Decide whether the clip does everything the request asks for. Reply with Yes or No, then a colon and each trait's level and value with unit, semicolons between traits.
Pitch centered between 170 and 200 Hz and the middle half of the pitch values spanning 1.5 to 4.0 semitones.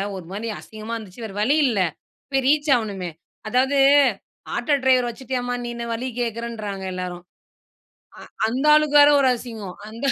No: high, 235 Hz; average, 3.5 semitones